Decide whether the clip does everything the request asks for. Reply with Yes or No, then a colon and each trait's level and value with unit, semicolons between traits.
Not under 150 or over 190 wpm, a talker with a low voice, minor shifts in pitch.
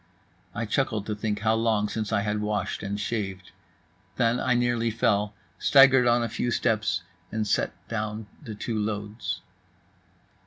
Yes: average, 155 wpm; low, 110 Hz; narrow, 2.0 semitones